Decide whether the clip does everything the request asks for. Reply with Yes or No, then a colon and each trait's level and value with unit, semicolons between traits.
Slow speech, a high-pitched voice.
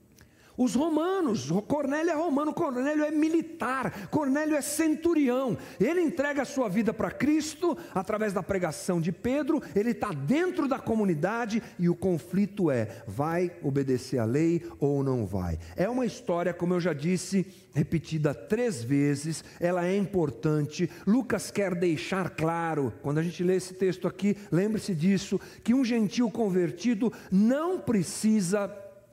No: average, 150 wpm; high, 195 Hz